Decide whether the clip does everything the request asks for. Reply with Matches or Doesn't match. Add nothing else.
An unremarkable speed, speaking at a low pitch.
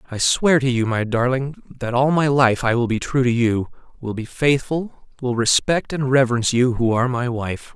Doesn't match